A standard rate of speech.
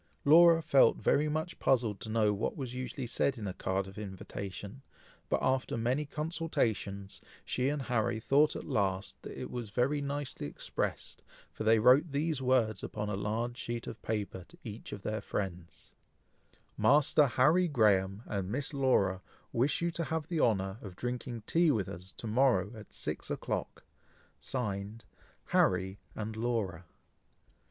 Yes: average, 160 wpm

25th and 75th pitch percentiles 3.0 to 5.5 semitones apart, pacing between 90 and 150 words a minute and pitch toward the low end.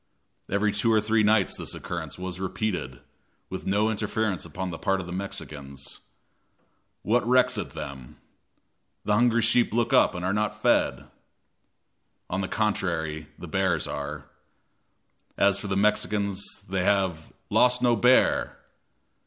Yes: average, 3.8 semitones; average, 145 wpm; low, 100 Hz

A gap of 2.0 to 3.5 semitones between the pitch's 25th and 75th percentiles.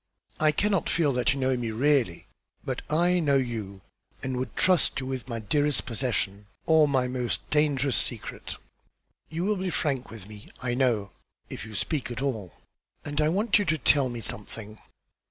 No: average, 4.8 semitones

